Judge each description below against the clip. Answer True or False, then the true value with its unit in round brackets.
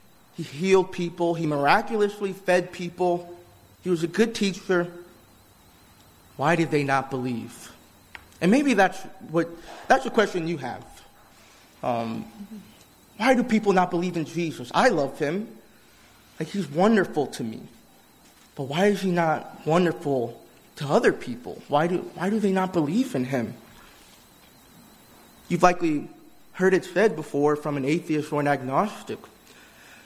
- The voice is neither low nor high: True (170 Hz)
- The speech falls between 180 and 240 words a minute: False (145 wpm)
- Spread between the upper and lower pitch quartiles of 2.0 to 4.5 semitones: False (4.9 semitones)